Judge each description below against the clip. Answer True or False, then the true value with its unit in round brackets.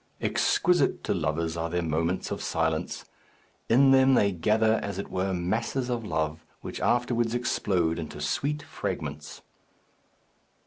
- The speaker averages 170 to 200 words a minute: False (135 wpm)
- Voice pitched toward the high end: False (95 Hz)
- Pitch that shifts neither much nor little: False (6.3 semitones)